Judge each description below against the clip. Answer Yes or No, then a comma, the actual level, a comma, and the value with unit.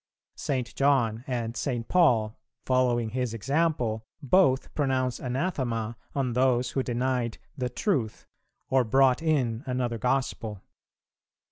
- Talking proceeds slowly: Yes, slow, 115 wpm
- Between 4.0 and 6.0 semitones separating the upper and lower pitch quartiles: No, narrow, 2.5 semitones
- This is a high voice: No, low, 125 Hz